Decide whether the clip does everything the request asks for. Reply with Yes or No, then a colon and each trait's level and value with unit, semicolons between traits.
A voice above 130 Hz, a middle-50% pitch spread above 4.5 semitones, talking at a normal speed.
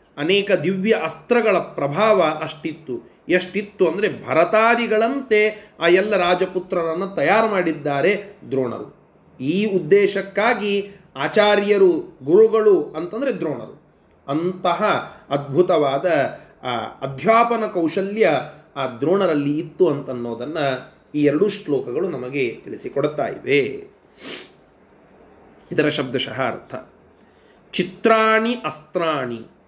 Yes: high, 190 Hz; wide, 5.5 semitones; average, 80 wpm